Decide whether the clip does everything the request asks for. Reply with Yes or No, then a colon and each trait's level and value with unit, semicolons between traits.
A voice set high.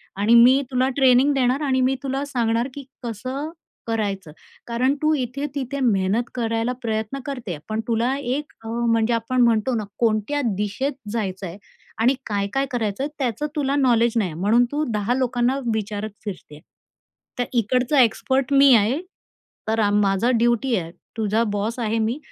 Yes: high, 235 Hz